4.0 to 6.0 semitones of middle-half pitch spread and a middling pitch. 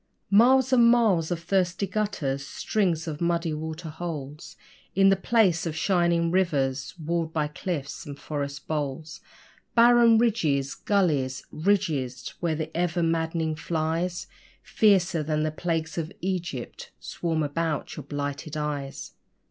No: average, 3.4 semitones; medium, 165 Hz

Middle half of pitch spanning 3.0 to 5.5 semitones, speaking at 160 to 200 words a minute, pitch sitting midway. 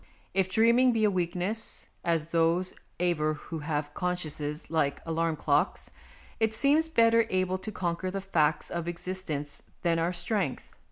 No: average, 3.5 semitones; average, 150 wpm; medium, 175 Hz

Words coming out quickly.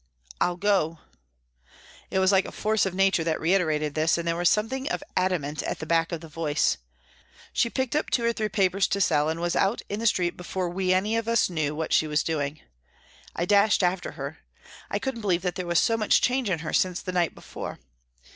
Yes: fast, 230 wpm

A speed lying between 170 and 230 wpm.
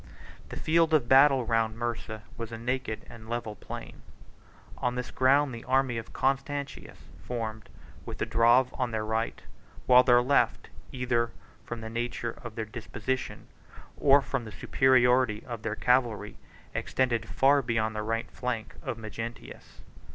No: average, 150 wpm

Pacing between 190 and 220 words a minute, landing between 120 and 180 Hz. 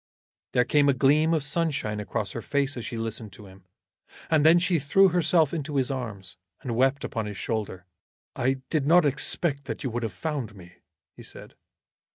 Yes: average, 195 wpm; low, 135 Hz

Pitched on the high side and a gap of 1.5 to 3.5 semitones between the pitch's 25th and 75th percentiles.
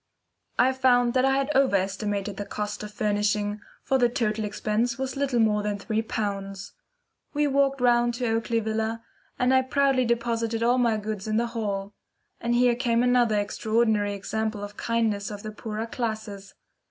Yes: high, 225 Hz; average, 2.8 semitones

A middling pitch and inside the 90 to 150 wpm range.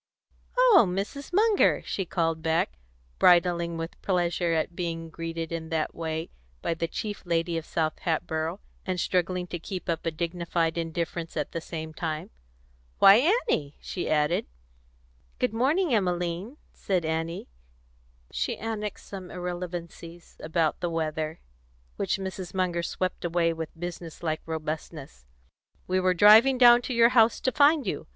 Yes: medium, 170 Hz; average, 145 wpm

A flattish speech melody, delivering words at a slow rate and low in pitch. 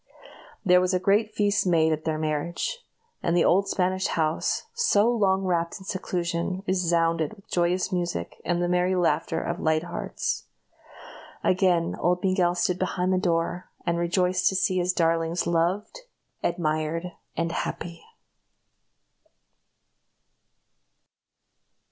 No: narrow, 1.9 semitones; slow, 130 wpm; medium, 180 Hz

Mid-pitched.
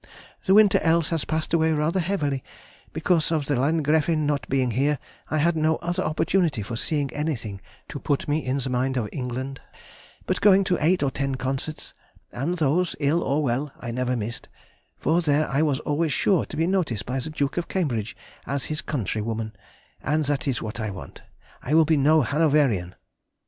Yes: medium, 145 Hz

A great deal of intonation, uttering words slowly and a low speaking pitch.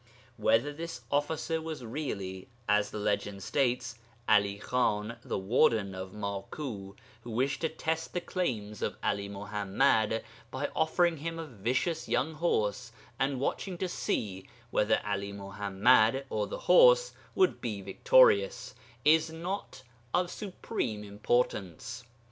Yes: wide, 7.7 semitones; slow, 130 wpm; low, 120 Hz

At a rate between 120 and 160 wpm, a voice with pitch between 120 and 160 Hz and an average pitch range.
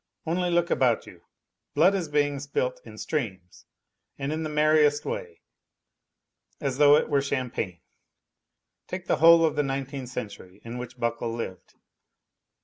Yes: average, 145 wpm; medium, 140 Hz; average, 4.3 semitones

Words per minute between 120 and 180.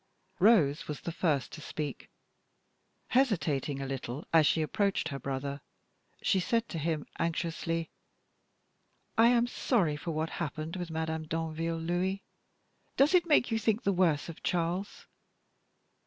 Yes: average, 140 wpm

